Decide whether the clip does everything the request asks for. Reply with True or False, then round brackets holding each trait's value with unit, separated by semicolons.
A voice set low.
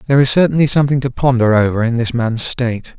True (125 Hz)